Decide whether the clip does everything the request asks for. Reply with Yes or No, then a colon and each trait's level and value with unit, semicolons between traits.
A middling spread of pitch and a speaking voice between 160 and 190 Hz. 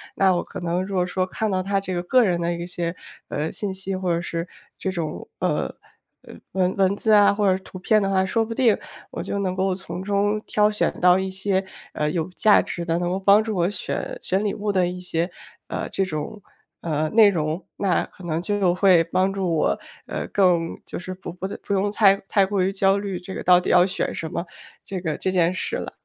No: narrow, 2.2 semitones; medium, 185 Hz